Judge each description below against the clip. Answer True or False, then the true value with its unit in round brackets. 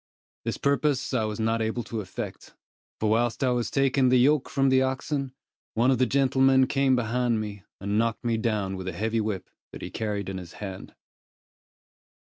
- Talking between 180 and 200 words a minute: True (190 wpm)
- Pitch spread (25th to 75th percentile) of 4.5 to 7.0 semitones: False (3.5 semitones)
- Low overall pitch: True (115 Hz)